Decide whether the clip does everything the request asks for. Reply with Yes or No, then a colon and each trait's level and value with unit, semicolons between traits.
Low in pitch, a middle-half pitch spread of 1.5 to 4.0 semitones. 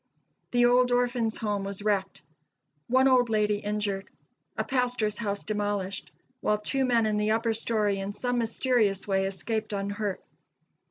No: high, 215 Hz; average, 3.0 semitones